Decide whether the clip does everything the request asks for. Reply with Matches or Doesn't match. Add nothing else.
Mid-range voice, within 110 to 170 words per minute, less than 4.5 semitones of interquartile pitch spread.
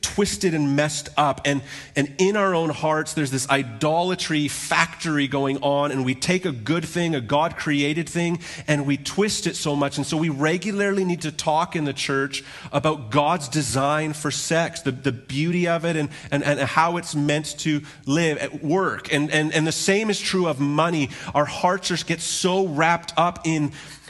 Doesn't match